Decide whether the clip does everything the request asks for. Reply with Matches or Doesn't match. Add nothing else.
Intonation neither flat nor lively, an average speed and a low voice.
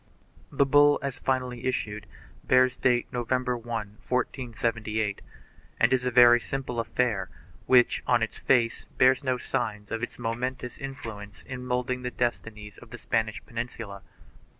Doesn't match